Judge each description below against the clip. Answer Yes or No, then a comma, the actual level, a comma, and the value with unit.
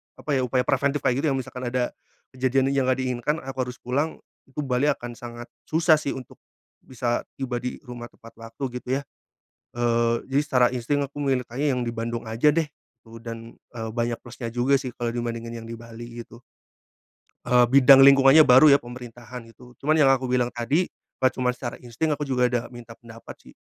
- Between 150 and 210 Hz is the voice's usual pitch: No, low, 125 Hz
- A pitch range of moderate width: No, narrow, 2.3 semitones